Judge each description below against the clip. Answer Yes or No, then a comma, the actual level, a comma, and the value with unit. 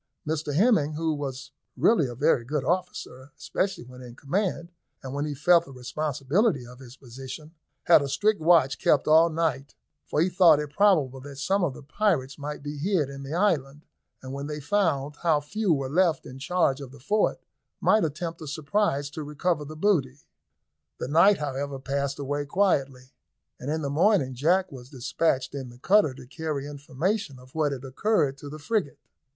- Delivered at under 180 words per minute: No, average, 190 wpm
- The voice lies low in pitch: No, medium, 145 Hz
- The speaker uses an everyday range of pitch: Yes, average, 3.9 semitones